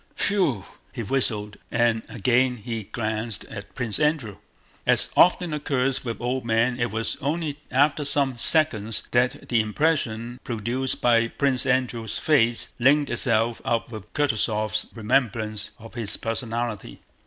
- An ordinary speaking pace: No, slow, 130 wpm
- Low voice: Yes, low, 120 Hz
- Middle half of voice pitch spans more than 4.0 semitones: No, average, 3.2 semitones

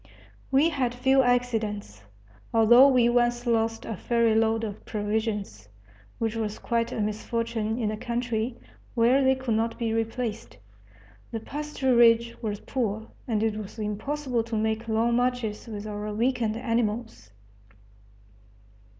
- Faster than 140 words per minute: No, slow, 135 wpm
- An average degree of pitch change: No, narrow, 2.0 semitones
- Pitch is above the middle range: Yes, high, 230 Hz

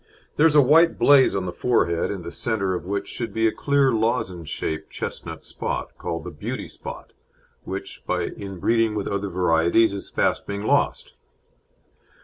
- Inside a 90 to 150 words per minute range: No, average, 170 wpm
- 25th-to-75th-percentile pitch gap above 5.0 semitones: No, average, 4.6 semitones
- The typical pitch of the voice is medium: No, low, 100 Hz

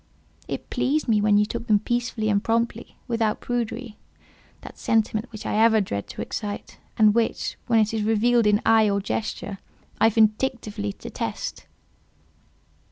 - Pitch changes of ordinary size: No, narrow, 1.9 semitones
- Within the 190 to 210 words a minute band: No, average, 150 wpm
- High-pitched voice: Yes, high, 220 Hz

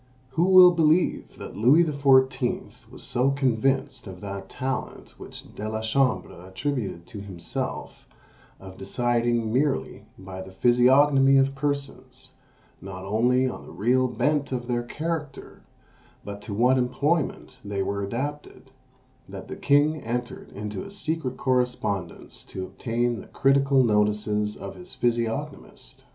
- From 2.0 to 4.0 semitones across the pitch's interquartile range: No, average, 4.7 semitones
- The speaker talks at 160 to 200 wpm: No, slow, 135 wpm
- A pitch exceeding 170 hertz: No, low, 125 Hz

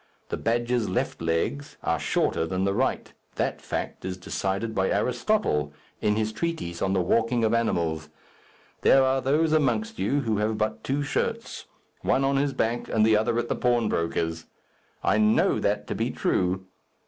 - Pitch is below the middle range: Yes, low, 110 Hz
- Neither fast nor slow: Yes, average, 170 wpm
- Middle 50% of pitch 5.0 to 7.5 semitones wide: Yes, wide, 5.6 semitones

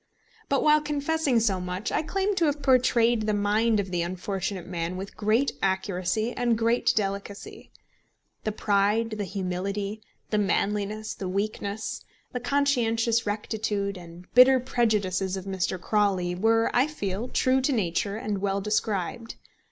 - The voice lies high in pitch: Yes, high, 210 Hz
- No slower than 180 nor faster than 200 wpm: No, average, 145 wpm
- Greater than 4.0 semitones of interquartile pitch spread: No, average, 3.4 semitones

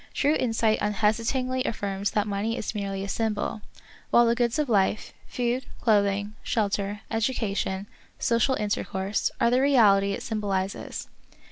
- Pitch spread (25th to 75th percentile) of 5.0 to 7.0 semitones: No, average, 2.9 semitones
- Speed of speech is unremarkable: Yes, average, 150 wpm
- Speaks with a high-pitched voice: Yes, high, 215 Hz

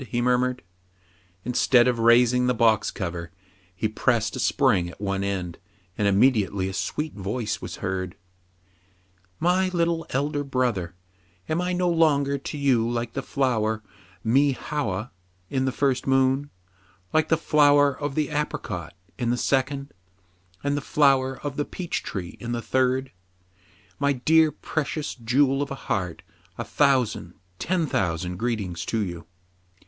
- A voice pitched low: Yes, low, 125 Hz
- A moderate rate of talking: Yes, average, 160 wpm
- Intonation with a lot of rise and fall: Yes, wide, 6.1 semitones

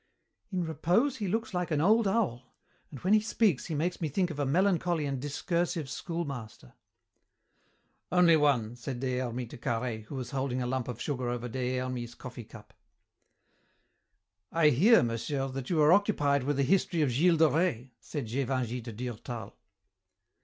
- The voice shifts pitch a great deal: Yes, wide, 5.7 semitones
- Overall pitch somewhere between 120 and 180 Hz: Yes, medium, 140 Hz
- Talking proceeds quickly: No, average, 175 wpm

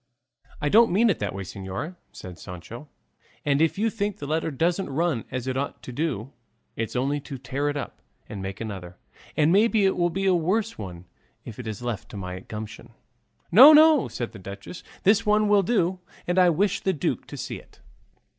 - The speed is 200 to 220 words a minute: Yes, fast, 205 wpm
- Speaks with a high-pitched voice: No, medium, 145 Hz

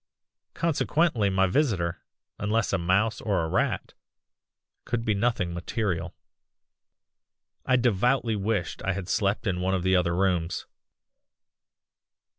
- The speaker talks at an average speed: No, slow, 120 wpm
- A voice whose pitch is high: No, low, 100 Hz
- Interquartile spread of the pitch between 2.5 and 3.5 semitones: No, average, 3.9 semitones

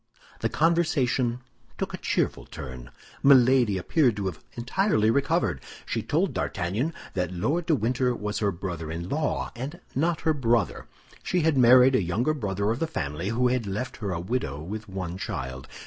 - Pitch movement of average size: No, wide, 6.7 semitones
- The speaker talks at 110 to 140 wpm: No, average, 175 wpm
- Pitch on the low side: Yes, low, 115 Hz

